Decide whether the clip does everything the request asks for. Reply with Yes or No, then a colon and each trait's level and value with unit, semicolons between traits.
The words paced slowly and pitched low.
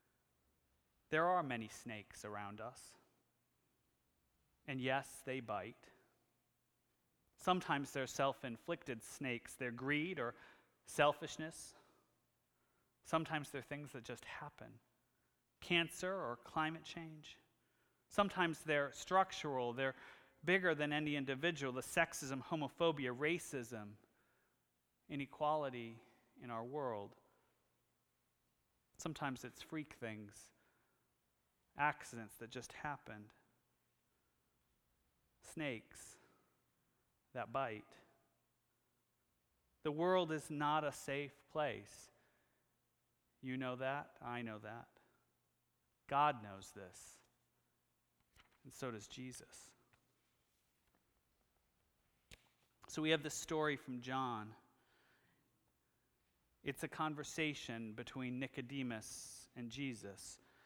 Yes: slow, 90 wpm; low, 130 Hz